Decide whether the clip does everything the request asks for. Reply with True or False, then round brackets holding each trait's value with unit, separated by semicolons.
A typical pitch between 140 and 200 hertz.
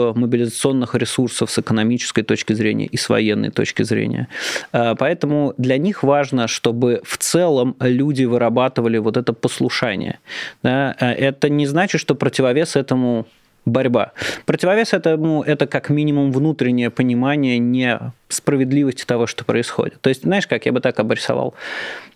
False (130 Hz)